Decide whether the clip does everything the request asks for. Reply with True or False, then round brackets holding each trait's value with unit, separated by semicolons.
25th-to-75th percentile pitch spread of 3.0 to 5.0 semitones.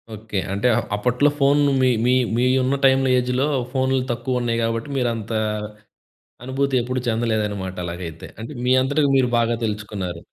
True (3.6 semitones)